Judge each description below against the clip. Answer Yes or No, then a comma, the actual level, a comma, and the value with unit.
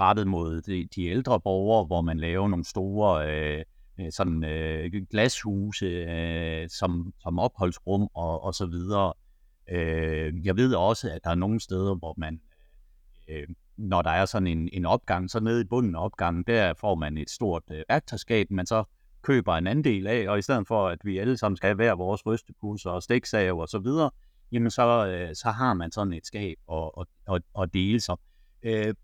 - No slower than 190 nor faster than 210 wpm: Yes, average, 195 wpm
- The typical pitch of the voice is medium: No, very low, 95 Hz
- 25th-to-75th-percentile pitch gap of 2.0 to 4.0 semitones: No, average, 4.6 semitones